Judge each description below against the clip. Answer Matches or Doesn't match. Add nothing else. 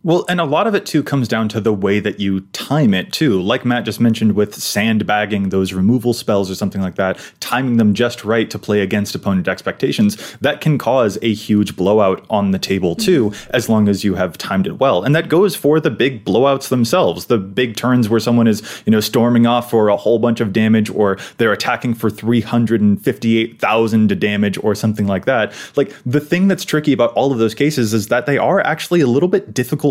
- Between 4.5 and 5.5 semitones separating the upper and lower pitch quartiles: Doesn't match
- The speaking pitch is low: Matches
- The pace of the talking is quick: Matches